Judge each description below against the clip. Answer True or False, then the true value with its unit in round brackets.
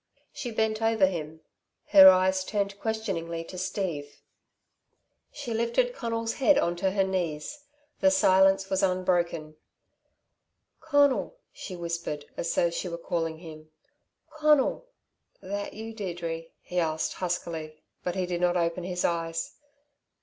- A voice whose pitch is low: False (185 Hz)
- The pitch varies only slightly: False (4.5 semitones)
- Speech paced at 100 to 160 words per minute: True (135 wpm)